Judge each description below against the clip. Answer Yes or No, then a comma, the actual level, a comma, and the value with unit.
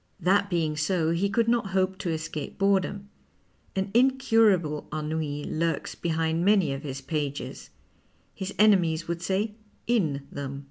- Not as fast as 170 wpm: Yes, average, 140 wpm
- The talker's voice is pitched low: No, medium, 170 Hz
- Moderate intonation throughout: Yes, average, 4.4 semitones